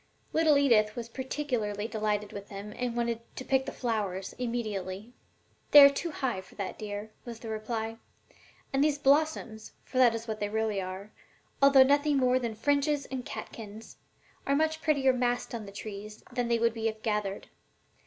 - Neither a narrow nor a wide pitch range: Yes, average, 4.0 semitones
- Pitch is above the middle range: Yes, high, 230 Hz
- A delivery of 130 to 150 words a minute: No, average, 180 wpm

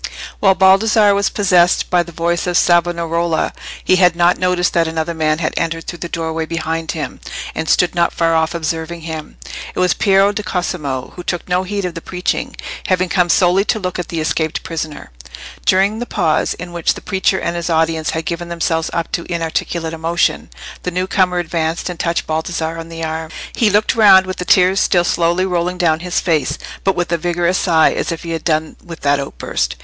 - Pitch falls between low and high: Yes, medium, 170 Hz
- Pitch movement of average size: No, narrow, 1.9 semitones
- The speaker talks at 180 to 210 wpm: Yes, fast, 205 wpm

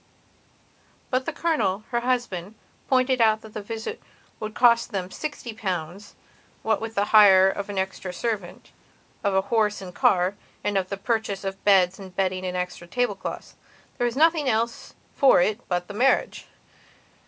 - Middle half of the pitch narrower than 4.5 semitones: Yes, average, 3.8 semitones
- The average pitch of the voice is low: No, high, 205 Hz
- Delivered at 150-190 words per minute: Yes, average, 170 wpm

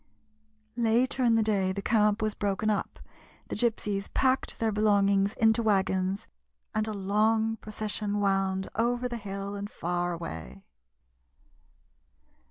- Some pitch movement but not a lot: No, narrow, 2.1 semitones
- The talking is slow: Yes, slow, 130 wpm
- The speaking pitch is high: Yes, high, 210 Hz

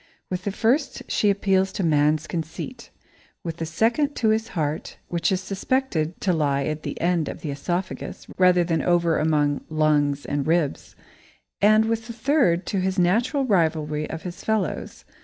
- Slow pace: No, average, 170 wpm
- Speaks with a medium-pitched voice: Yes, medium, 175 Hz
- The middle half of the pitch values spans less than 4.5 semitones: No, average, 5.2 semitones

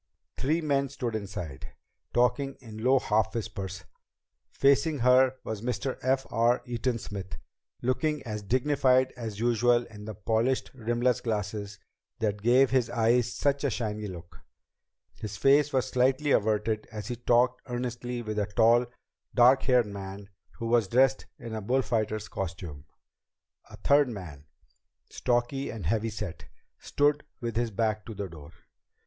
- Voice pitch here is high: No, low, 120 Hz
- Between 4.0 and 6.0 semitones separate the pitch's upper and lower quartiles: No, average, 3.4 semitones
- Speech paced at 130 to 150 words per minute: Yes, average, 145 wpm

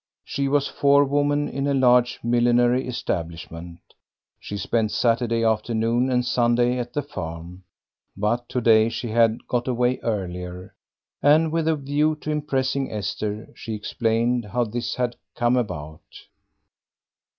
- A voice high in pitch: No, low, 120 Hz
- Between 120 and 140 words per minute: Yes, slow, 135 wpm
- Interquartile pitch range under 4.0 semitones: Yes, average, 3.4 semitones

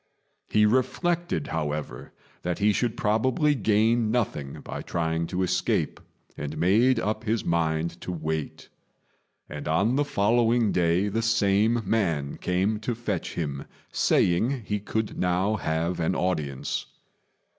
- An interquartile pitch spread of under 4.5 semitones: No, average, 5.3 semitones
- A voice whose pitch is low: Yes, low, 100 Hz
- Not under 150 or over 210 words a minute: No, slow, 135 wpm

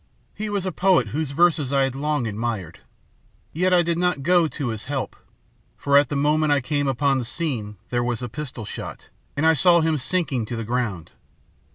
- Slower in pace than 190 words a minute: No, fast, 205 wpm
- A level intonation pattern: No, average, 5.0 semitones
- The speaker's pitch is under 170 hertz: Yes, medium, 140 Hz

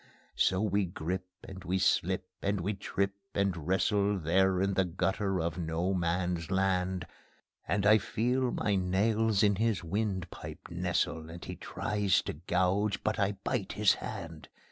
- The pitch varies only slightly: Yes, narrow, 2.3 semitones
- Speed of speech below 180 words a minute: Yes, average, 160 wpm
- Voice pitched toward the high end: No, very low, 95 Hz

